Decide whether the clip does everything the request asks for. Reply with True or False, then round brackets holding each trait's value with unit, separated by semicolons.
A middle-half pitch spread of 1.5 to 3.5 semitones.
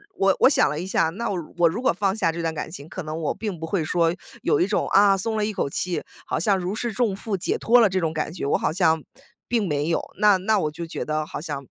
False (4.1 semitones)